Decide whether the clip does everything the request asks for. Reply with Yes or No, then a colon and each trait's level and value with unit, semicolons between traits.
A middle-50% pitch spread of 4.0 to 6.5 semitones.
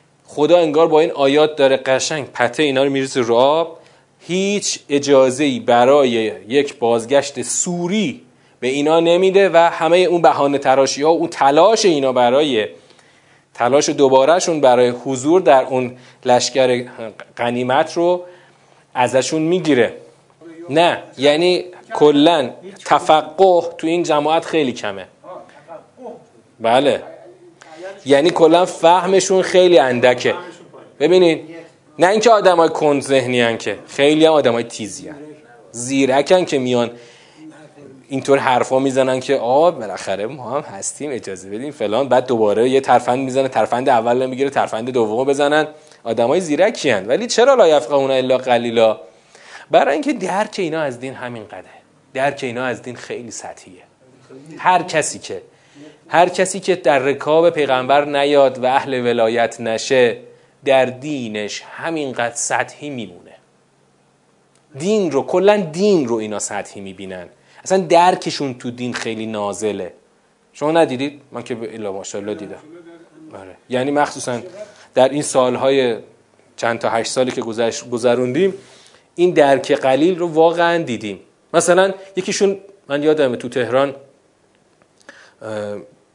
Yes: average, 5.2 semitones